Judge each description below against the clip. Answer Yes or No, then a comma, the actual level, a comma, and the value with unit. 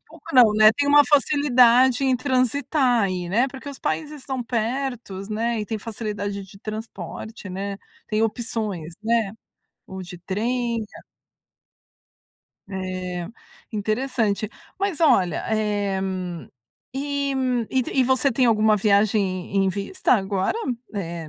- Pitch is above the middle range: Yes, high, 220 Hz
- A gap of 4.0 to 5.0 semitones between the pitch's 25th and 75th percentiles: Yes, average, 4.5 semitones